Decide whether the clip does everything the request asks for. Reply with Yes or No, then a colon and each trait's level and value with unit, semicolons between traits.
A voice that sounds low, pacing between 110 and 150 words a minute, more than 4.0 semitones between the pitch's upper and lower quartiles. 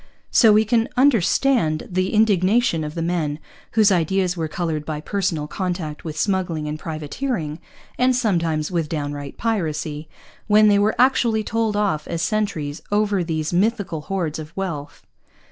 No: medium, 180 Hz; average, 145 wpm; wide, 5.5 semitones